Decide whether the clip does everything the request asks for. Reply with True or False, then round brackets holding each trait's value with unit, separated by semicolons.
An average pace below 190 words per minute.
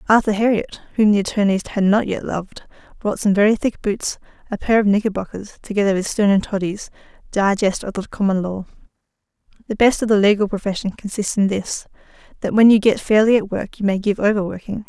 False (195 wpm)